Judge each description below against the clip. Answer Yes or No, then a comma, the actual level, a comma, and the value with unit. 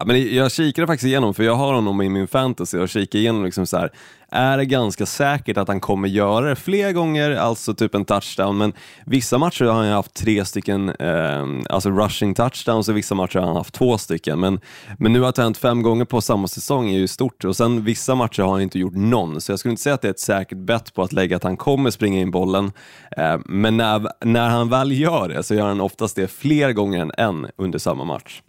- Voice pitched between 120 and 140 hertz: No, low, 110 Hz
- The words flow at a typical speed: No, fast, 250 wpm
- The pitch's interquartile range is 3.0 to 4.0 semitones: No, average, 4.4 semitones